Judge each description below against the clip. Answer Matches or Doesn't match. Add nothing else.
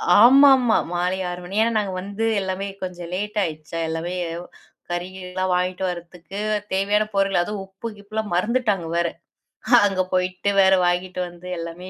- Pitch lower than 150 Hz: Doesn't match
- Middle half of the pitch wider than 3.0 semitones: Doesn't match